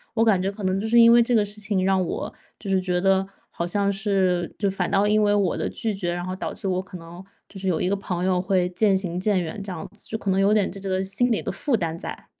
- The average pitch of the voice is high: Yes, high, 195 Hz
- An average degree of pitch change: No, narrow, 2.1 semitones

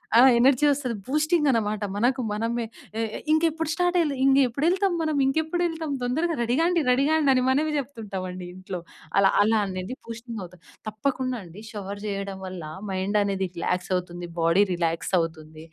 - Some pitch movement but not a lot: No, wide, 7.5 semitones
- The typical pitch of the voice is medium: No, high, 235 Hz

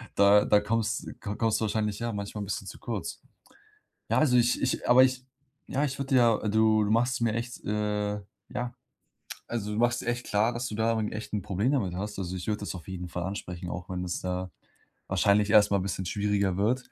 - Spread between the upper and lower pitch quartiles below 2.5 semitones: No, average, 2.8 semitones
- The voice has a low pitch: Yes, low, 105 Hz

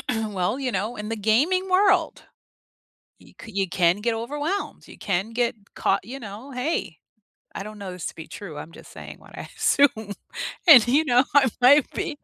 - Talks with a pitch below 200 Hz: No, high, 230 Hz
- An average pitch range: No, wide, 6.0 semitones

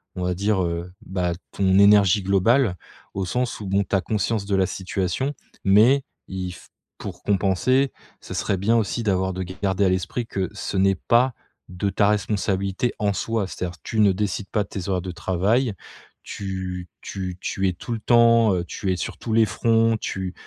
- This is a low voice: Yes, low, 100 Hz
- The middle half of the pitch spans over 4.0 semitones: No, average, 2.8 semitones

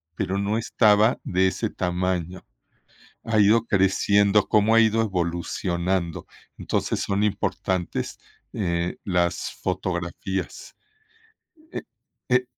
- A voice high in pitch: No, very low, 95 Hz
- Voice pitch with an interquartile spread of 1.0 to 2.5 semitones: No, average, 2.9 semitones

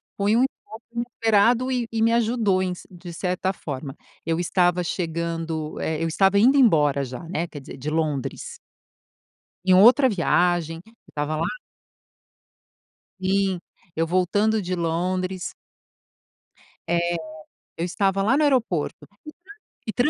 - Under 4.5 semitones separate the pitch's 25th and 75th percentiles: No, average, 4.8 semitones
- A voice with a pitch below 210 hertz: Yes, medium, 185 Hz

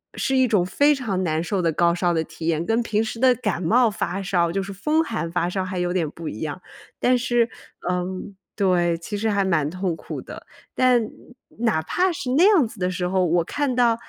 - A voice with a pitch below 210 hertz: Yes, high, 190 Hz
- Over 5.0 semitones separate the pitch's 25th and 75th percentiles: Yes, wide, 5.4 semitones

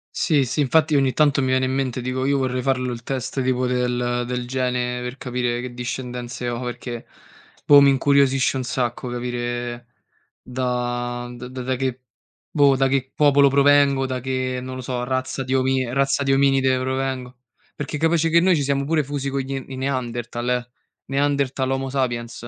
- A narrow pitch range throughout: Yes, narrow, 1.8 semitones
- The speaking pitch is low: Yes, low, 130 Hz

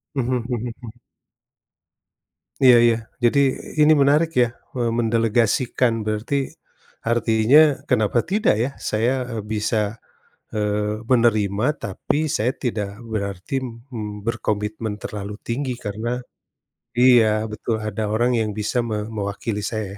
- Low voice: Yes, low, 115 Hz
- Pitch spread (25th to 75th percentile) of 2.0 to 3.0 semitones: Yes, narrow, 2.6 semitones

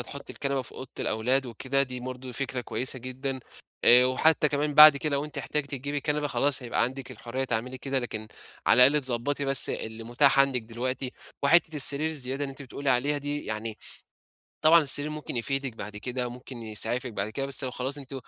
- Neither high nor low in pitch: No, low, 130 Hz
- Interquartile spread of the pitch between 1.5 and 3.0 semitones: Yes, narrow, 2.5 semitones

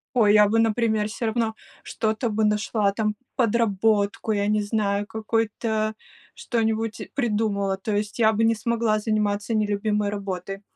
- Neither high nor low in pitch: No, high, 215 Hz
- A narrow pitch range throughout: Yes, narrow, 1.4 semitones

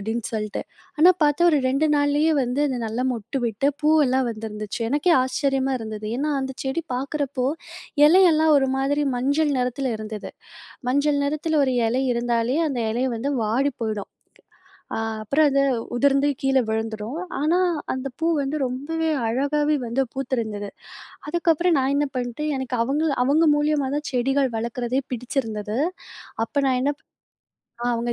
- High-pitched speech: Yes, very high, 270 Hz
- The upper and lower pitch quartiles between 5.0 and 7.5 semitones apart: No, average, 3.7 semitones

